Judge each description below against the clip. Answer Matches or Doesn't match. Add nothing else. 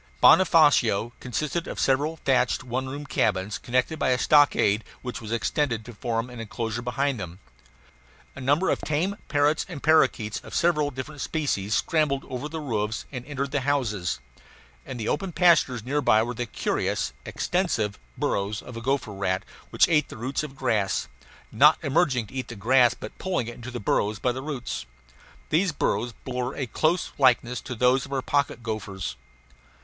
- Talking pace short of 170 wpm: Doesn't match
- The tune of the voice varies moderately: Matches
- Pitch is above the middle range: Doesn't match